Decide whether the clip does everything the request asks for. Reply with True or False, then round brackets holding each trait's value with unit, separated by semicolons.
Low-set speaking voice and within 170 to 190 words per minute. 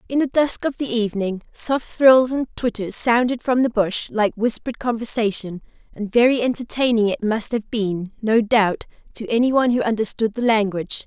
False (230 Hz; 180 wpm)